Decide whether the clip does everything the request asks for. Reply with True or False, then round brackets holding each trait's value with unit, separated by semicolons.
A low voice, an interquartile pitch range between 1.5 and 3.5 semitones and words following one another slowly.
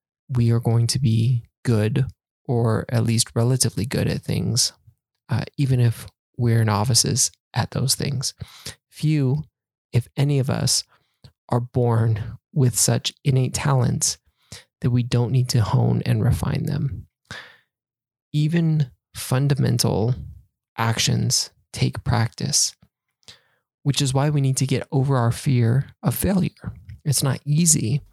True (125 Hz; 2.9 semitones; 130 wpm)